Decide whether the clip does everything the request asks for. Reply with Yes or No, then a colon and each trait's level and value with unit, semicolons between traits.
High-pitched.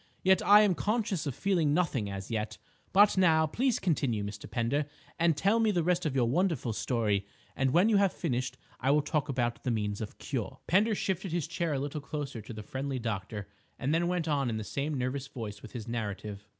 No: medium, 140 Hz